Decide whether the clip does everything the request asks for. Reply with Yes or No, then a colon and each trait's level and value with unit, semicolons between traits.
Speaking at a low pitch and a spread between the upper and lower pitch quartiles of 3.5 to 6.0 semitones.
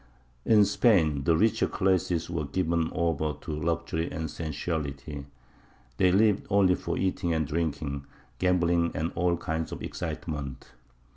No: very low, 85 Hz; average, 2.8 semitones